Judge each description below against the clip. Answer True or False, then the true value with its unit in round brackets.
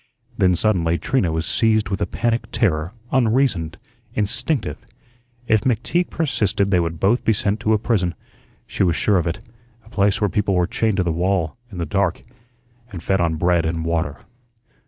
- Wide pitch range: False (4.5 semitones)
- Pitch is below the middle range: True (95 Hz)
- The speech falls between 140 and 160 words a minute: False (180 wpm)